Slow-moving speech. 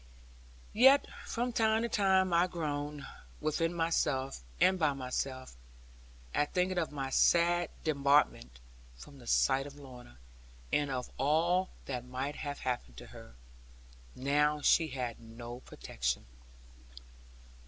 Yes: slow, 125 wpm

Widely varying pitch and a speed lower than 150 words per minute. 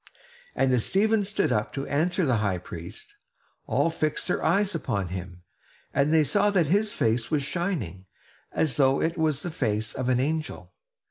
No: wide, 7.6 semitones; average, 180 wpm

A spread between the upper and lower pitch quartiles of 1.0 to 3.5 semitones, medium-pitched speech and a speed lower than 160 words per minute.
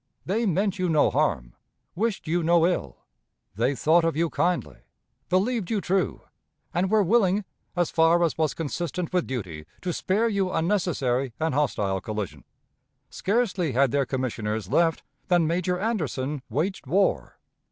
No: wide, 5.5 semitones; medium, 170 Hz; average, 150 wpm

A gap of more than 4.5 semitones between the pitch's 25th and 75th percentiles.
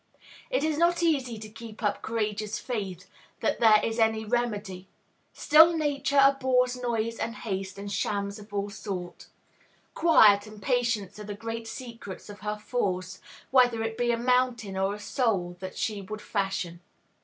No: average, 3.4 semitones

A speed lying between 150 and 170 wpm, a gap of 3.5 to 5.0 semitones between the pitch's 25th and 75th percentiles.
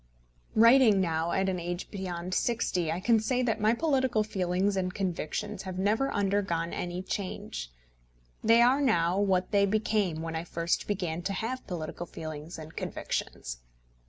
Yes: average, 160 wpm; average, 4.1 semitones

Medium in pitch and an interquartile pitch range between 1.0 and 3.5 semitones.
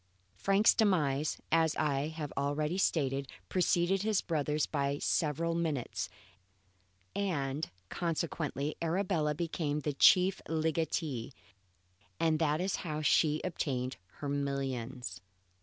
Yes: medium, 155 Hz; average, 3.1 semitones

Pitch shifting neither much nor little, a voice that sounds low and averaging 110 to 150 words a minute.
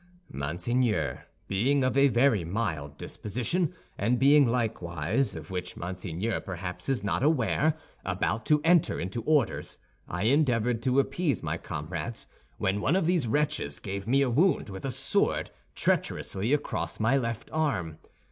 No: wide, 6.9 semitones; low, 115 Hz; average, 145 wpm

